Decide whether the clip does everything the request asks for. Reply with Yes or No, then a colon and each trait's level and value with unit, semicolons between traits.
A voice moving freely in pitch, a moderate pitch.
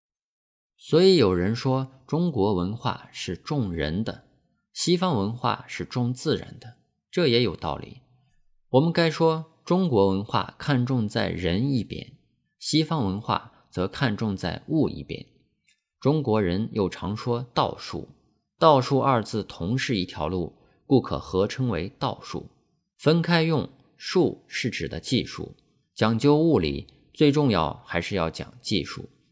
No: wide, 6.5 semitones; low, 125 Hz